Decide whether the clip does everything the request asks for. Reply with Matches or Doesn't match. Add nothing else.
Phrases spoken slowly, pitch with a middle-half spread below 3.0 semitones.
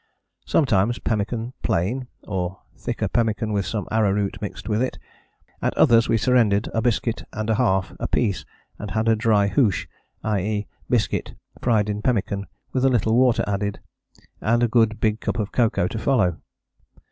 Doesn't match